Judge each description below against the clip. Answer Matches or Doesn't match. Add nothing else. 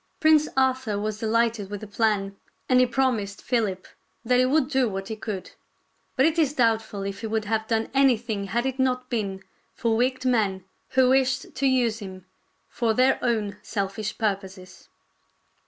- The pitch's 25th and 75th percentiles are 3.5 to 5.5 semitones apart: Matches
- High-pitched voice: Matches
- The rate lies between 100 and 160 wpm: Doesn't match